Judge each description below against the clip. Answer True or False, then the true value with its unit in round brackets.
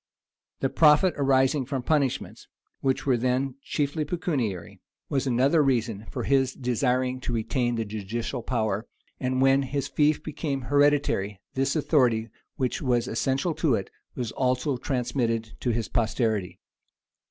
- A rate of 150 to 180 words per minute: False (140 wpm)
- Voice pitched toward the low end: True (130 Hz)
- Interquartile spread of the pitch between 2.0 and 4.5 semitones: True (3.1 semitones)